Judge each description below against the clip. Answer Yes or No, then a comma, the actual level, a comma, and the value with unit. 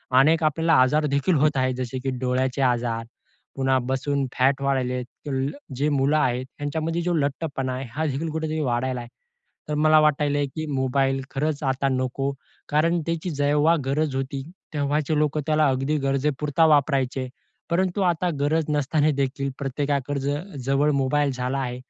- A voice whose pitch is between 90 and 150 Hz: Yes, medium, 140 Hz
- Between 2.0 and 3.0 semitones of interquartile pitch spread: Yes, narrow, 2.5 semitones